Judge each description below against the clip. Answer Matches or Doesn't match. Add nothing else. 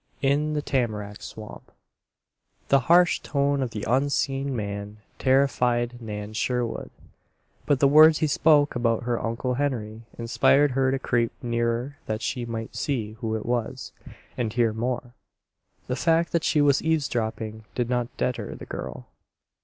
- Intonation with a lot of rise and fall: Doesn't match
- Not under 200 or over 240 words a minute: Doesn't match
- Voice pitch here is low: Matches